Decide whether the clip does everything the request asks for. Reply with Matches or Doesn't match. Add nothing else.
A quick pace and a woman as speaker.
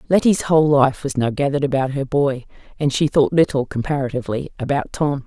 Doesn't match